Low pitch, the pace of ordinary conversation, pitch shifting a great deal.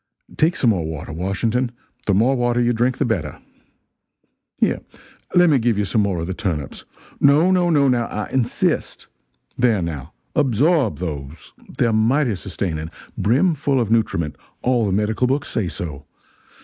Yes: low, 115 Hz; average, 160 wpm; wide, 6.0 semitones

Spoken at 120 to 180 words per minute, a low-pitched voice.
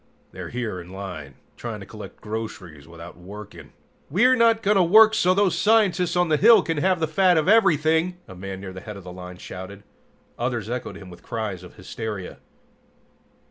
No: average, 190 wpm; low, 120 Hz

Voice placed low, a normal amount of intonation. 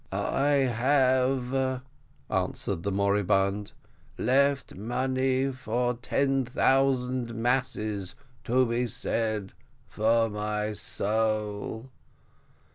Yes: low, 120 Hz; average, 3.6 semitones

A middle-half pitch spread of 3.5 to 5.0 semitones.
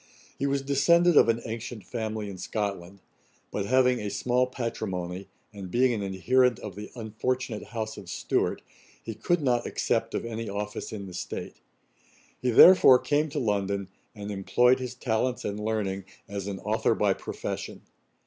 Yes: average, 4.0 semitones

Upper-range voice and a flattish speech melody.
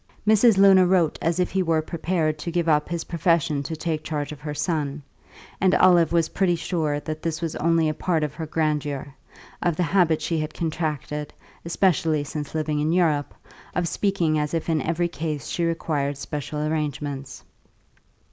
No: medium, 160 Hz; narrow, 2.2 semitones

